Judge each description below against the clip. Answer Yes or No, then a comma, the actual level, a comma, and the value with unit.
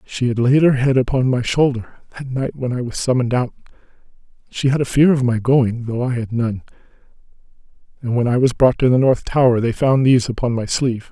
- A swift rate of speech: Yes, fast, 210 wpm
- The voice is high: No, low, 125 Hz